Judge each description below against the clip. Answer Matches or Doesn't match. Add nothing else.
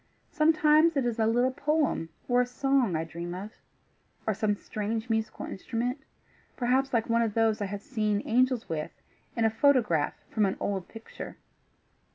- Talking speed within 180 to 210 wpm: Doesn't match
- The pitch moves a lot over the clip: Doesn't match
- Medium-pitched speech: Doesn't match